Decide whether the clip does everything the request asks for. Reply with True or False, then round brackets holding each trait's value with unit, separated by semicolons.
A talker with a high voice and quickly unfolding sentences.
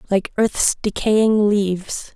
False (205 Hz; 110 wpm)